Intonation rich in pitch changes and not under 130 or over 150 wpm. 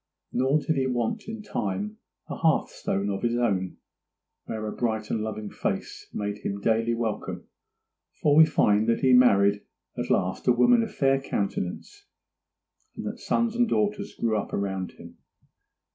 No: wide, 5.7 semitones; average, 165 wpm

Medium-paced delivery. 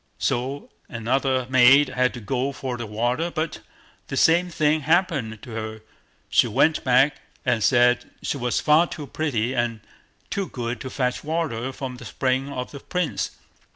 Yes: average, 165 wpm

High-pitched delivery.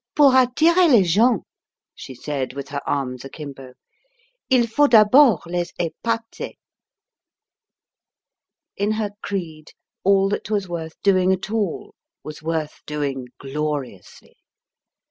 No: medium, 180 Hz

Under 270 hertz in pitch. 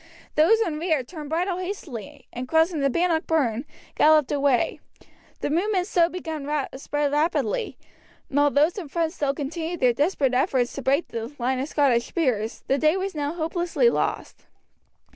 No: very high, 300 Hz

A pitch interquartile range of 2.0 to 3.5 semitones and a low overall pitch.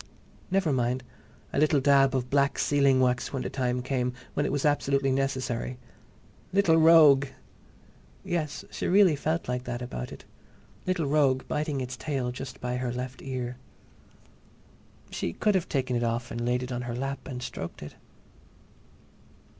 Yes: narrow, 2.6 semitones; low, 130 Hz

